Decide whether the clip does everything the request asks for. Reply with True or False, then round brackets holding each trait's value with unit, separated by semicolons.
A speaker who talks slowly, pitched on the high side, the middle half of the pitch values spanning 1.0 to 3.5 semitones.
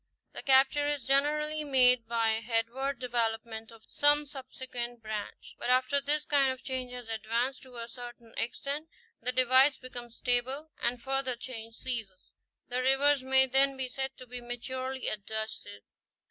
False (160 wpm; 255 Hz; 2.5 semitones)